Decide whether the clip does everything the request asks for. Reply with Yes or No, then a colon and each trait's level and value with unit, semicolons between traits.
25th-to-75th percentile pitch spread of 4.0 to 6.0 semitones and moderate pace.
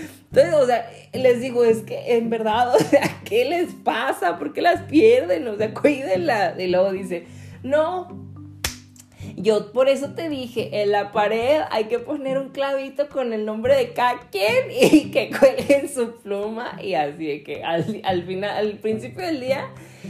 Yes: wide, 5.6 semitones; average, 175 wpm